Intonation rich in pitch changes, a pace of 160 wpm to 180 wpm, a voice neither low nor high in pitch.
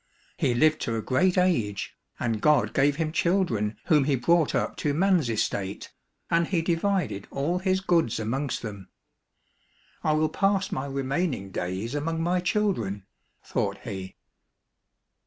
No: wide, 7.4 semitones; average, 150 wpm; medium, 145 Hz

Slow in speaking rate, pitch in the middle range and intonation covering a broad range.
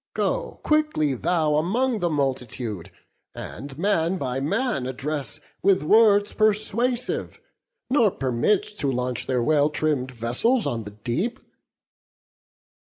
Yes: slow, 115 wpm; medium, 155 Hz; wide, 8.7 semitones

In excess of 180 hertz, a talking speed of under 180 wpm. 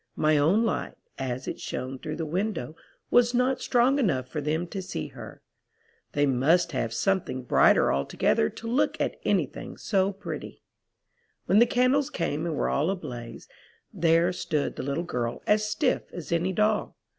No: medium, 170 Hz; average, 170 wpm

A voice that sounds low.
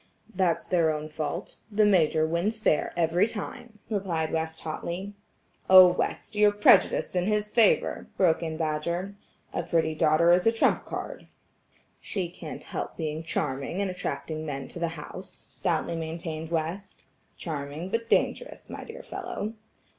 No: medium, 170 Hz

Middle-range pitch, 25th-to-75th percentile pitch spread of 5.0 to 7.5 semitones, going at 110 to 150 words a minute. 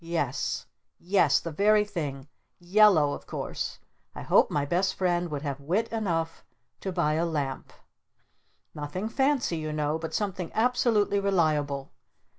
Yes: medium, 170 Hz; average, 5.3 semitones; average, 140 wpm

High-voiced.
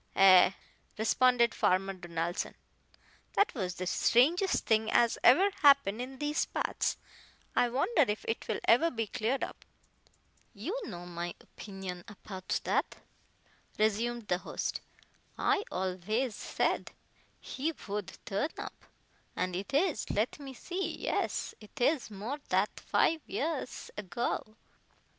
Yes: high, 220 Hz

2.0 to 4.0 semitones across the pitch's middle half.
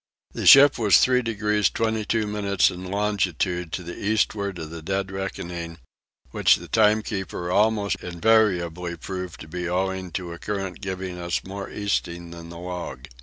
Yes: average, 3.1 semitones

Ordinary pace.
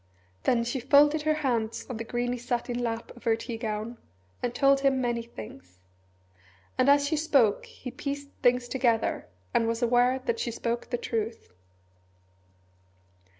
Yes: average, 155 wpm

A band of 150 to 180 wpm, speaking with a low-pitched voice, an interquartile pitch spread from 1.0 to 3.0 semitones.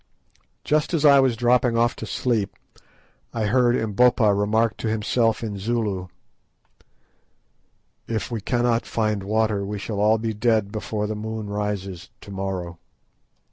No: average, 140 wpm; low, 110 Hz; narrow, 2.5 semitones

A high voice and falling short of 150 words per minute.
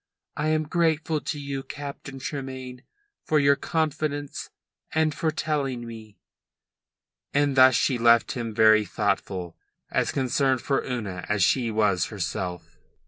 No: low, 130 Hz; slow, 135 wpm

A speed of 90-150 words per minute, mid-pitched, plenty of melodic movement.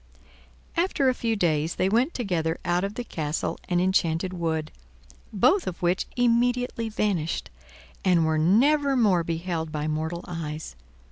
Yes: average, 140 wpm; medium, 180 Hz; wide, 6.2 semitones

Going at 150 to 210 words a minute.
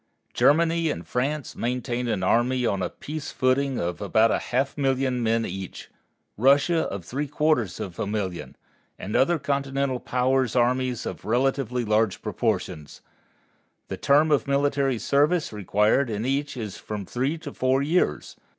Yes: average, 155 wpm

